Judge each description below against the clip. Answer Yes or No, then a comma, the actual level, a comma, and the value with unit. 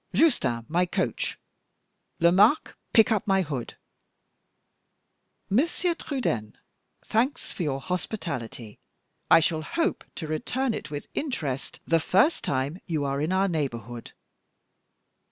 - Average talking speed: No, slow, 120 wpm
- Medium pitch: Yes, medium, 170 Hz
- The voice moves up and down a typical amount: No, wide, 7.8 semitones